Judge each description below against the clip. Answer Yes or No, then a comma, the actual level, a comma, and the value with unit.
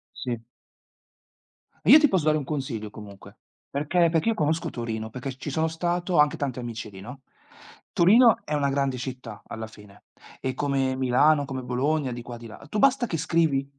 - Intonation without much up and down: No, average, 4.8 semitones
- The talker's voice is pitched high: No, medium, 140 Hz